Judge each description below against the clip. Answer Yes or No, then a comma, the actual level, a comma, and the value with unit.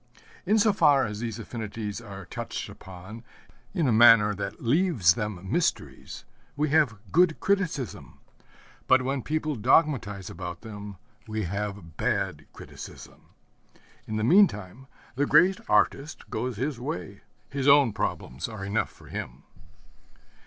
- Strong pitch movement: Yes, wide, 6.0 semitones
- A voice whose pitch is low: Yes, low, 115 Hz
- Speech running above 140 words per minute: No, slow, 135 wpm